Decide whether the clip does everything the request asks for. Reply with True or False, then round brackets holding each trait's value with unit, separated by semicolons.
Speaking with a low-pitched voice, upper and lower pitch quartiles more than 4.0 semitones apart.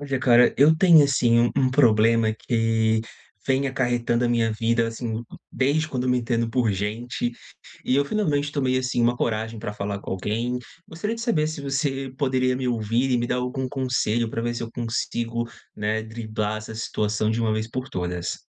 False (120 Hz; 2.9 semitones)